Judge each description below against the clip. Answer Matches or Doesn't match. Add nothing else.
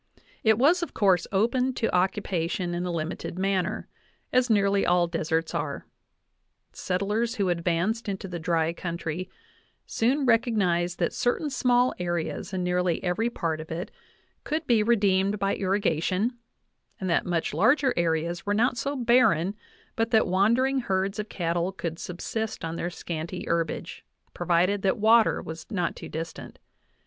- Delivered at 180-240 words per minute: Doesn't match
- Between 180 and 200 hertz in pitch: Matches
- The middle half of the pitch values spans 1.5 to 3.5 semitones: Doesn't match